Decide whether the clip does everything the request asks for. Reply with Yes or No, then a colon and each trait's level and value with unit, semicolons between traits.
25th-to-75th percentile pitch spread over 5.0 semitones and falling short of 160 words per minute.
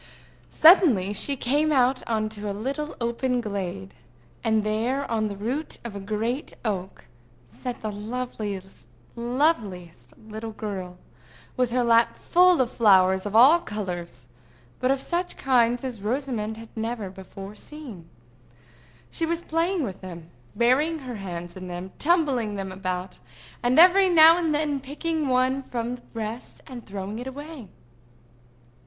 Yes: wide, 5.4 semitones; average, 140 wpm